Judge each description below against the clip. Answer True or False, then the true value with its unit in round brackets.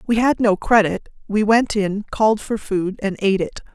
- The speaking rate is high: True (210 wpm)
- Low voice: False (210 Hz)